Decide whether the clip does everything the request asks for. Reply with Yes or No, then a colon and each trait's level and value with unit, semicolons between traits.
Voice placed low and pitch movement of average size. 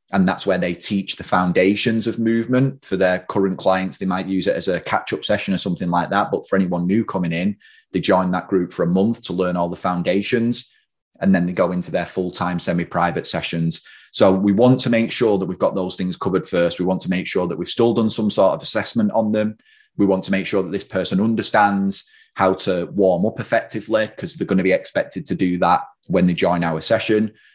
Yes: very low, 95 Hz; average, 3.2 semitones